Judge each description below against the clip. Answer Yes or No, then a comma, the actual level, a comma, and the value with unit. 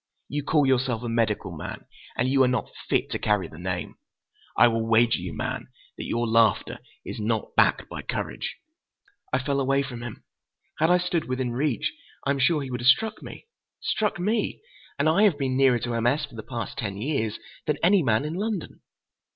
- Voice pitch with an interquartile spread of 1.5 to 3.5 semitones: No, average, 4.5 semitones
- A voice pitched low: Yes, low, 130 Hz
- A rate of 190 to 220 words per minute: Yes, average, 200 wpm